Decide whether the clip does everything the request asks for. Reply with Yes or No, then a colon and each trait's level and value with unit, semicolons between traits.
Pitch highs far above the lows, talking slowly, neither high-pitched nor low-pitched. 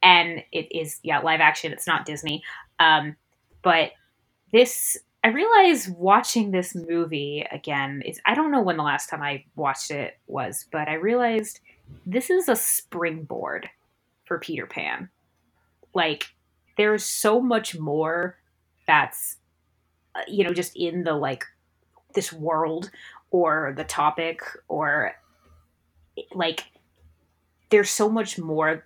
Yes: wide, 5.8 semitones; slow, 130 wpm; medium, 160 Hz